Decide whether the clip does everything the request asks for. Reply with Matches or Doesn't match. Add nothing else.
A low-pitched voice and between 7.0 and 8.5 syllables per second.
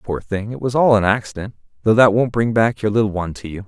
Doesn't match